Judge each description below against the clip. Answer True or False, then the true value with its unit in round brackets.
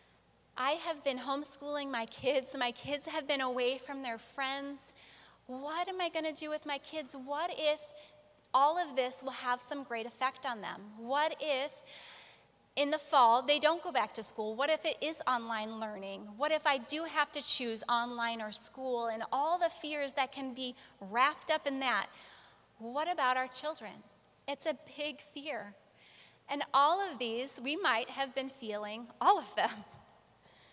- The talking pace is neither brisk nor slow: True (180 wpm)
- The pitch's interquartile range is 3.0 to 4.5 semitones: True (3.4 semitones)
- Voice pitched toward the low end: False (275 Hz)